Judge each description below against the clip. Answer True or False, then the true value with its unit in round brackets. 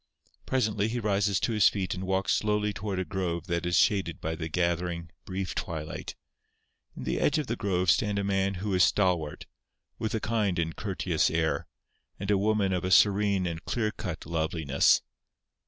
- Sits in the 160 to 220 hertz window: False (95 Hz)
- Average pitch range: True (3.3 semitones)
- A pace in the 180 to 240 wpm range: True (185 wpm)